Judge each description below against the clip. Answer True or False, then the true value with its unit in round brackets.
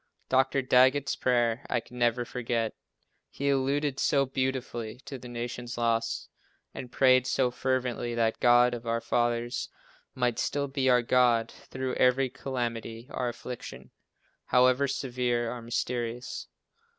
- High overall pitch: False (125 Hz)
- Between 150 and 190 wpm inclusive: False (140 wpm)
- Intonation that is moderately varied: False (1.7 semitones)